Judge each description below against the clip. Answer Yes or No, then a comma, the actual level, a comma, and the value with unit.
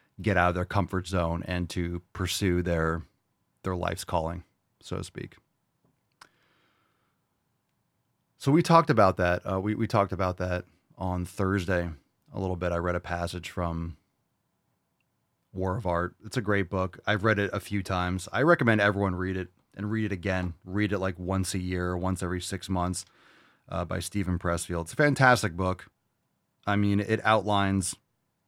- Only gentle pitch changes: Yes, narrow, 2.3 semitones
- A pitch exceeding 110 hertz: No, very low, 95 Hz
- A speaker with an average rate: Yes, average, 170 wpm